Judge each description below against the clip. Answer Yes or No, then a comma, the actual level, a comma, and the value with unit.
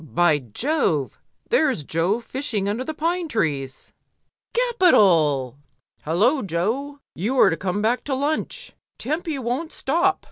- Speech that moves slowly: Yes, slow, 130 wpm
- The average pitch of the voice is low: No, high, 235 Hz